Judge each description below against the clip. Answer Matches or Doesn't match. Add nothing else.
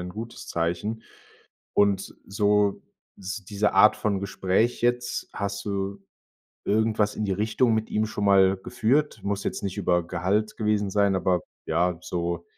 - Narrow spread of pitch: Matches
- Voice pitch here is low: Matches